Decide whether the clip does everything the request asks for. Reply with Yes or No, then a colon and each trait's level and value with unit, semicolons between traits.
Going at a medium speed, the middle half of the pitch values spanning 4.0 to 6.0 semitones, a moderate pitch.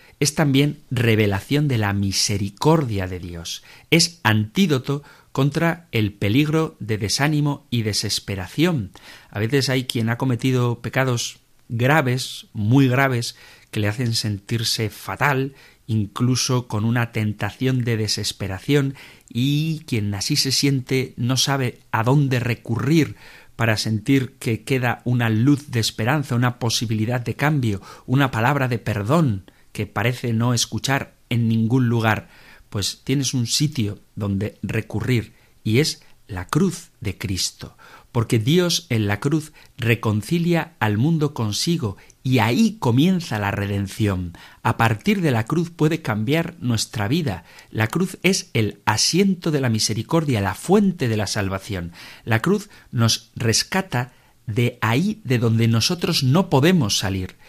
No: average, 135 wpm; average, 4.6 semitones; low, 120 Hz